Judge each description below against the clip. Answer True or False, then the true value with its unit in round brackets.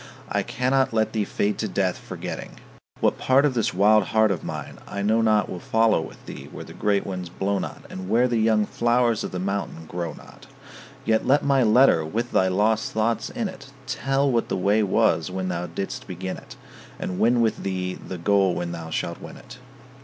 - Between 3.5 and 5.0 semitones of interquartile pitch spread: True (4.0 semitones)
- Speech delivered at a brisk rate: True (210 wpm)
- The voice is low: True (105 Hz)